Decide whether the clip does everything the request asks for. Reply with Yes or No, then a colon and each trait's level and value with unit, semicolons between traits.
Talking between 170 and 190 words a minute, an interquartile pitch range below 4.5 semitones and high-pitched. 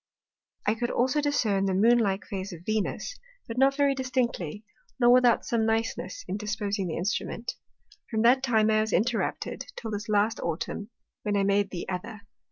Yes: average, 175 wpm; average, 3.2 semitones; high, 220 Hz